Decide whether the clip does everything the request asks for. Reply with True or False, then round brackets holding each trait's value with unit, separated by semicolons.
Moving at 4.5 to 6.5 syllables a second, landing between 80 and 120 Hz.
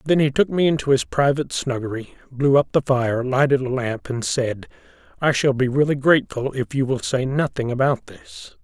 False (5.2 syllables/s; 135 Hz)